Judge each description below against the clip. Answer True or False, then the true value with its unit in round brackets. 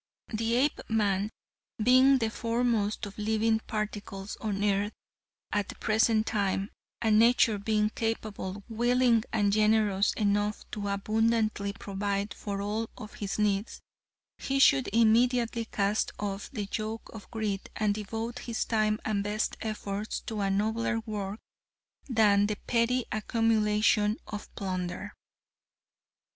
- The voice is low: False (215 Hz)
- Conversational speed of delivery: False (130 wpm)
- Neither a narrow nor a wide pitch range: False (1.8 semitones)